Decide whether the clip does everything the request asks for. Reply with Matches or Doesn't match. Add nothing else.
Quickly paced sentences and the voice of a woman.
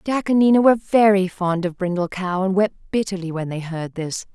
Matches